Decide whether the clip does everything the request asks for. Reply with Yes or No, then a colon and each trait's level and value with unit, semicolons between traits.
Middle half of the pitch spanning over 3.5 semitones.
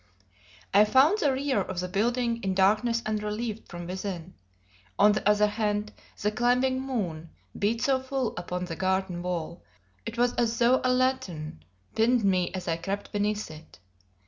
Yes: average, 4.6 semitones